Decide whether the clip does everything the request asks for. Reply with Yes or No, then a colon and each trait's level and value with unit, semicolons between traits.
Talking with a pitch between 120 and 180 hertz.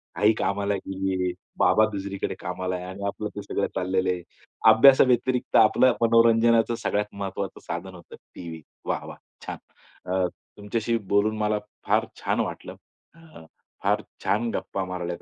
No: low, 100 Hz